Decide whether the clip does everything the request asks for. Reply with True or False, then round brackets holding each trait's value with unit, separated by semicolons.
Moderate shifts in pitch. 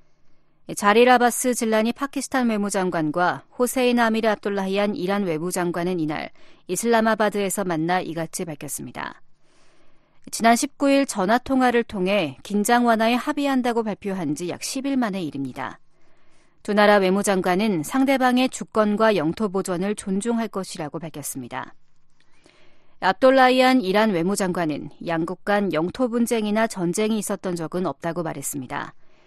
True (5.0 semitones)